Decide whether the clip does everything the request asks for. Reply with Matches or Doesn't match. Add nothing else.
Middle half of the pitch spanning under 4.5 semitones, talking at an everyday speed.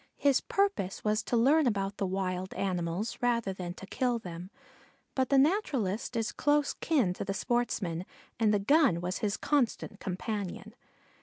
Doesn't match